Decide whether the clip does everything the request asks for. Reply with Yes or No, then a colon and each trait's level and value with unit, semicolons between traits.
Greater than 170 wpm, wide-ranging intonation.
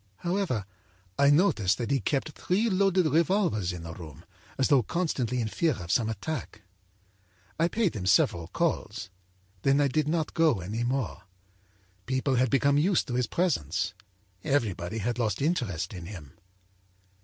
No: average, 155 wpm; wide, 7.8 semitones